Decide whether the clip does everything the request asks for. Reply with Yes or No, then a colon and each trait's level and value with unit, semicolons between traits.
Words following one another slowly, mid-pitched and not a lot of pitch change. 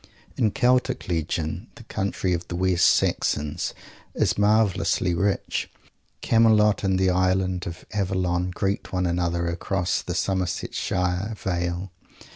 No: slow, 120 wpm; very low, 95 Hz; narrow, 2.1 semitones